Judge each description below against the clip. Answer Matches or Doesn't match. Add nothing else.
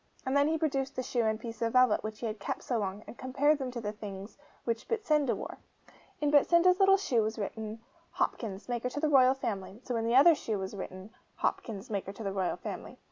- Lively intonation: Doesn't match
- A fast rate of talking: Matches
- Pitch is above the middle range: Matches